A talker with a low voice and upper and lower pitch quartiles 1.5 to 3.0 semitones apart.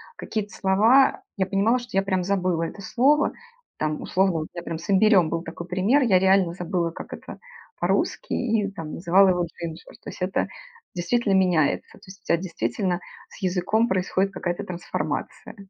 No: medium, 185 Hz; narrow, 2.6 semitones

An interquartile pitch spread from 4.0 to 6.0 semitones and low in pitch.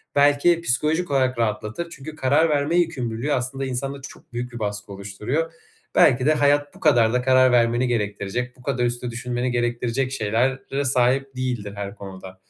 No: average, 3.2 semitones; low, 125 Hz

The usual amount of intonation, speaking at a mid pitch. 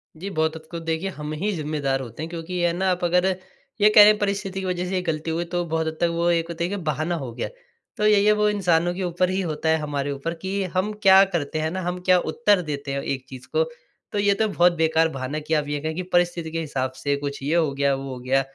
Yes: average, 3.4 semitones; medium, 165 Hz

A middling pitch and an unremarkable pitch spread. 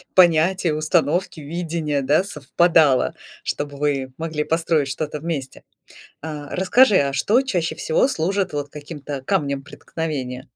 Yes: medium, 155 Hz; average, 3.3 semitones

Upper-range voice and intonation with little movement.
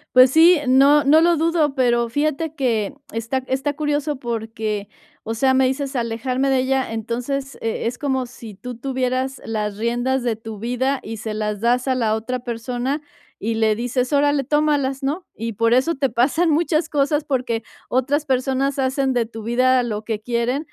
No: very high, 255 Hz; average, 3.2 semitones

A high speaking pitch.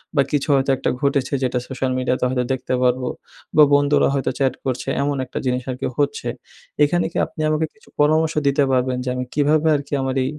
No: medium, 140 Hz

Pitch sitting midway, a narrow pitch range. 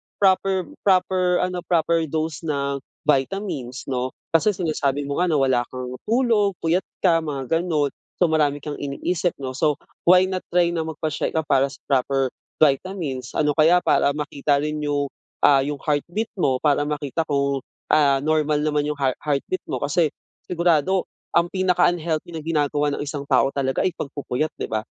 No: medium, 150 Hz; average, 3.7 semitones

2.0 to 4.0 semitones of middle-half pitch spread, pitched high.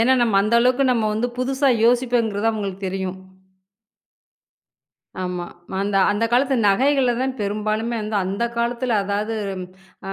Yes: average, 3.5 semitones; high, 225 Hz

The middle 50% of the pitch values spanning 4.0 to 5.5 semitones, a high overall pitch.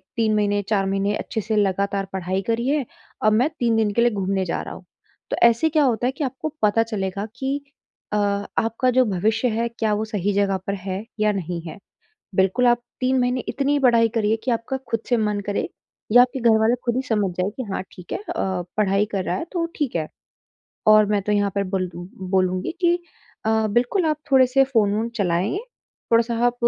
No: average, 3.5 semitones; high, 220 Hz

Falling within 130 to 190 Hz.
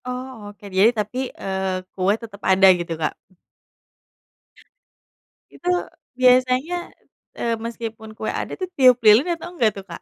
No: high, 225 Hz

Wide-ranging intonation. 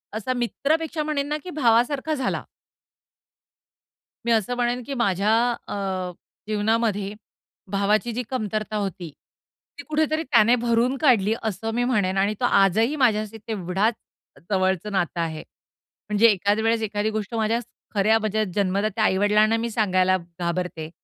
No: average, 3.5 semitones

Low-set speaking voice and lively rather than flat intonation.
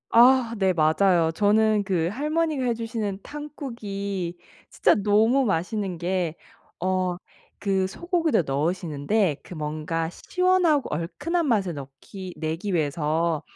No: high, 195 Hz; wide, 5.8 semitones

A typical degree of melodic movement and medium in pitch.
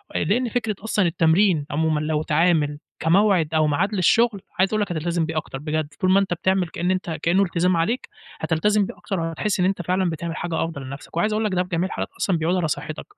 Yes: average, 3.3 semitones; medium, 175 Hz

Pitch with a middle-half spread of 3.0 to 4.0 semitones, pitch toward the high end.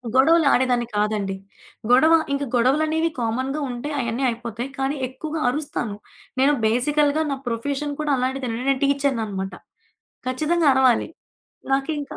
Yes: average, 3.6 semitones; very high, 265 Hz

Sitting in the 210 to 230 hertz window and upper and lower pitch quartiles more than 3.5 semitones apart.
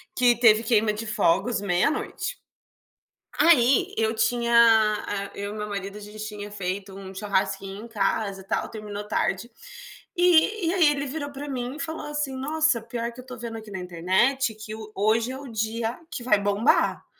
Yes: high, 225 Hz; average, 4.2 semitones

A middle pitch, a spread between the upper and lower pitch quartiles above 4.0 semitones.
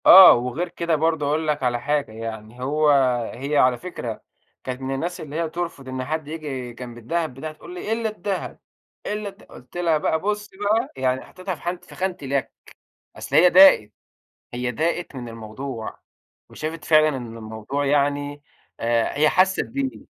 Yes: medium, 150 Hz; wide, 5.6 semitones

